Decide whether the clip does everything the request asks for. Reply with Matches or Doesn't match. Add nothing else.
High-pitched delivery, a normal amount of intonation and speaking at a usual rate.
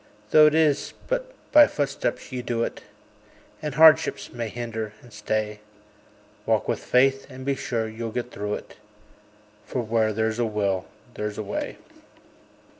Doesn't match